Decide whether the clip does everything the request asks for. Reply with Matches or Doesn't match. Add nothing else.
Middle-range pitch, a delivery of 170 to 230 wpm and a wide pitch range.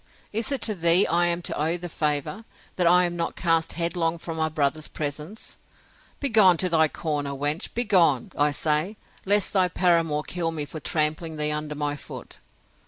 Doesn't match